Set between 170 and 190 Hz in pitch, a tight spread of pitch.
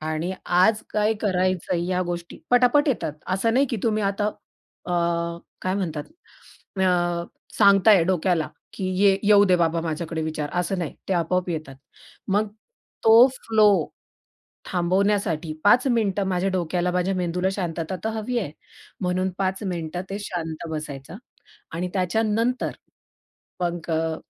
No: medium, 185 Hz; average, 3.1 semitones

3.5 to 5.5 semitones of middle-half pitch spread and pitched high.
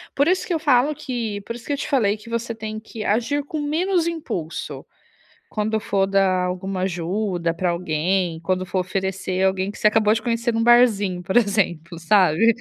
Yes: average, 4.3 semitones; high, 210 Hz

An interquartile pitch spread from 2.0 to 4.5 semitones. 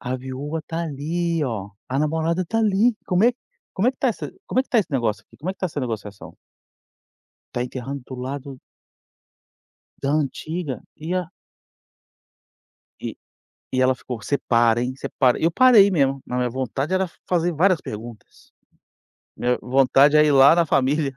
No: average, 5.0 semitones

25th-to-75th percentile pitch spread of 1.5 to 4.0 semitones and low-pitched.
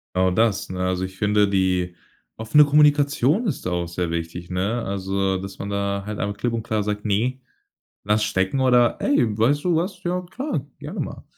No: wide, 5.4 semitones; low, 105 Hz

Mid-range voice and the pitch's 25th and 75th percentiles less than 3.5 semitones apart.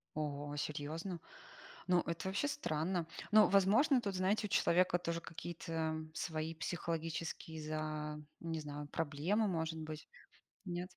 Yes: medium, 165 Hz; average, 2.9 semitones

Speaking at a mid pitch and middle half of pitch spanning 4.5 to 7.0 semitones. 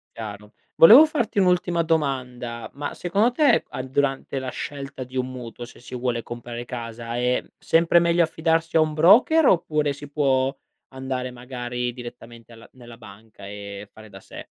No: low, 130 Hz; average, 5.2 semitones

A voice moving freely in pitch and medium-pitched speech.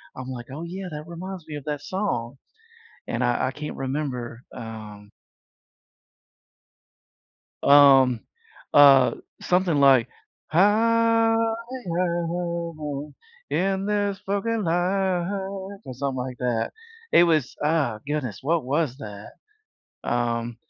Yes: wide, 6.4 semitones; medium, 145 Hz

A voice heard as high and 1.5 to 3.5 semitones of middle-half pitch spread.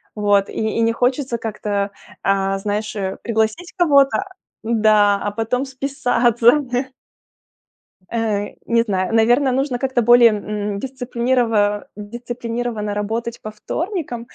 Yes: high, 230 Hz; average, 3.0 semitones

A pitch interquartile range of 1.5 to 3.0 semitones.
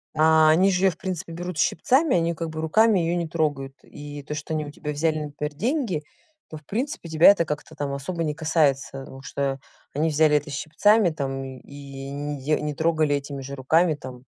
Yes: average, 2.7 semitones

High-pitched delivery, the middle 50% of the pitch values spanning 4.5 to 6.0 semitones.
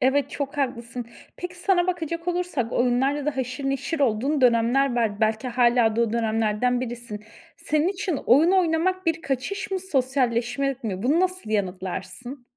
Yes: very high, 260 Hz; wide, 5.5 semitones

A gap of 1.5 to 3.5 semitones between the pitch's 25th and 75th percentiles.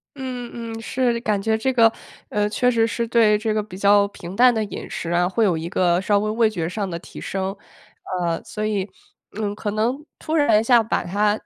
Yes: average, 2.9 semitones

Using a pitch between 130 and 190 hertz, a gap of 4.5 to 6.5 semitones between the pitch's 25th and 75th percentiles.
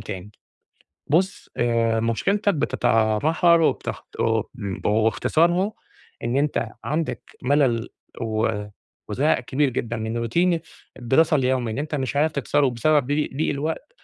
Yes: low, 135 Hz; wide, 5.4 semitones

